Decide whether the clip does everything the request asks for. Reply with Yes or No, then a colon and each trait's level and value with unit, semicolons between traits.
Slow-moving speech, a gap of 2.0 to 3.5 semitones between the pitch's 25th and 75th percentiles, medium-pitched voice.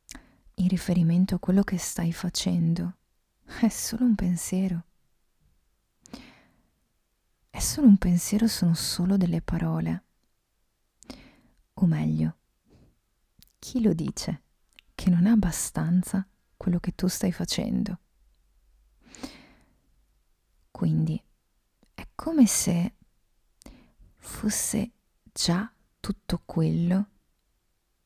Yes: slow, 90 wpm; average, 3.1 semitones; medium, 180 Hz